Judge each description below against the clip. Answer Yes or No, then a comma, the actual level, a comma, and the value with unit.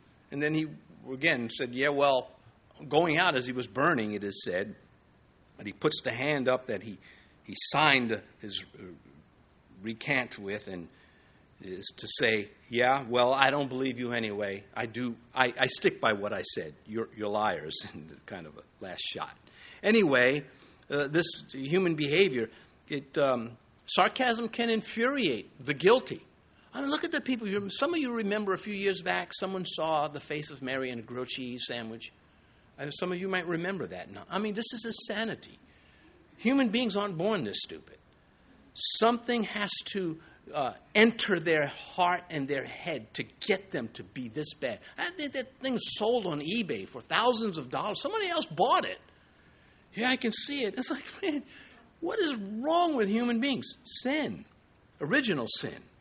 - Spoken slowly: No, average, 170 wpm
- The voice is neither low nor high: Yes, medium, 170 Hz